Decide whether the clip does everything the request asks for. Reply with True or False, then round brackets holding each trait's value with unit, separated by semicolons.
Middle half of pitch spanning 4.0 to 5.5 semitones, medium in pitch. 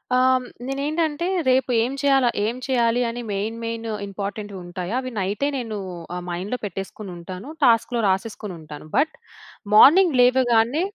False (4.6 semitones; 230 Hz)